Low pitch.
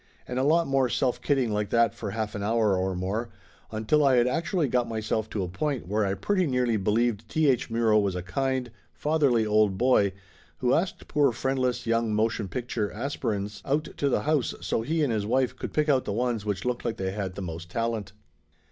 Yes: low, 115 Hz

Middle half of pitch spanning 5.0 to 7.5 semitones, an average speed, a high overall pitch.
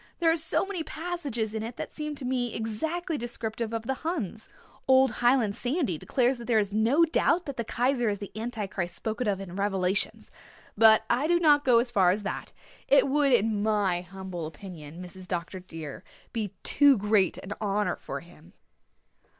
Yes: average, 5.3 semitones; average, 190 wpm; high, 225 Hz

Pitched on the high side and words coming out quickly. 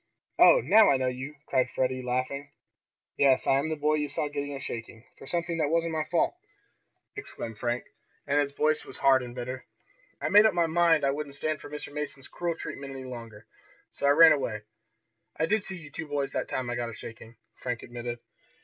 No: medium, 140 Hz; fast, 210 wpm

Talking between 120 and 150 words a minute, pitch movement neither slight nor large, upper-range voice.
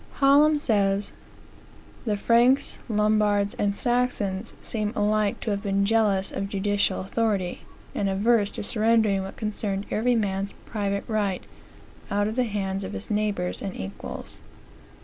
No: average, 140 wpm; narrow, 2.0 semitones; high, 205 Hz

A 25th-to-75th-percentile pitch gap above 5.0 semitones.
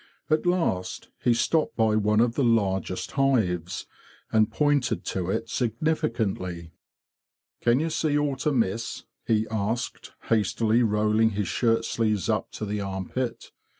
No: average, 3.5 semitones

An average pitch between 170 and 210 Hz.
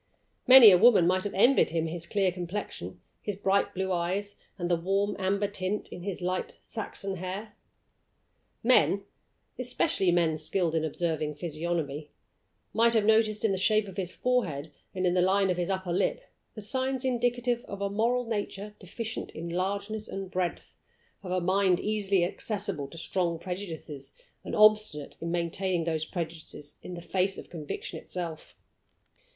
Yes: medium, 185 Hz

